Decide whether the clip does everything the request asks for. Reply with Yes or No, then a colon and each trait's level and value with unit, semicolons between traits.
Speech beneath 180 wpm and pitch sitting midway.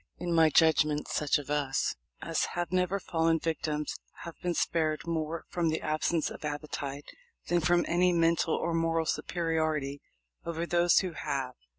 Yes: average, 160 wpm; medium, 165 Hz